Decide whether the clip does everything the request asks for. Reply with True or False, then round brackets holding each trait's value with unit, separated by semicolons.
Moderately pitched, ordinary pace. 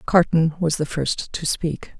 True (160 Hz; 180 wpm)